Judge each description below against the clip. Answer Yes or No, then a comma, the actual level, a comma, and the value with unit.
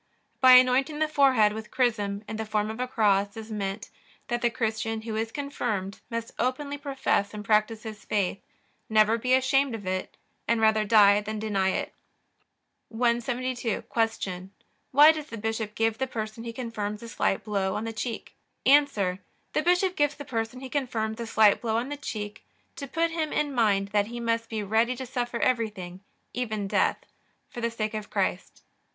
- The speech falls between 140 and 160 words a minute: No, average, 185 wpm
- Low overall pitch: No, high, 225 Hz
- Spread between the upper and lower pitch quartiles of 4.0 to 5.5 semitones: No, average, 3.1 semitones